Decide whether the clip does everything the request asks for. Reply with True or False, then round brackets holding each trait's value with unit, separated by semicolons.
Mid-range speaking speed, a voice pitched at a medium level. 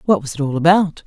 False (280 wpm; 160 Hz)